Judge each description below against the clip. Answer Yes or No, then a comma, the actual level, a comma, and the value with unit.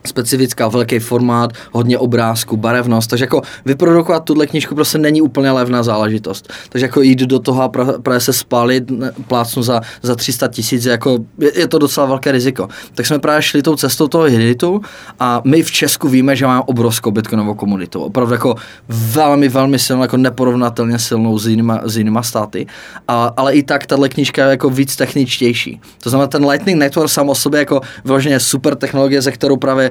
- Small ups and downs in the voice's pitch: No, average, 3.0 semitones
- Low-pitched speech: Yes, low, 130 Hz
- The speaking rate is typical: No, fast, 185 wpm